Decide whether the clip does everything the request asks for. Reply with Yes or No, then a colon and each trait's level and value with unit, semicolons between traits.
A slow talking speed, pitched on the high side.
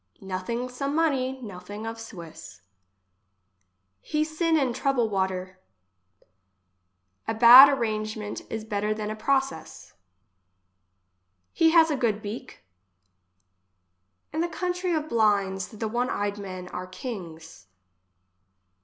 Yes: slow, 110 wpm; high, 220 Hz